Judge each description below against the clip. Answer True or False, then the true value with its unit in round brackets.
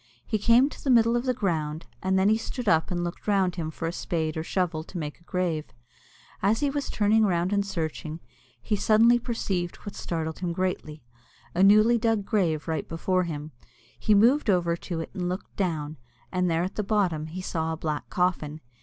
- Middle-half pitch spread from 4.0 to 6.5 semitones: True (4.5 semitones)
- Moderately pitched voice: True (180 Hz)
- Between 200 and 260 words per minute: True (205 wpm)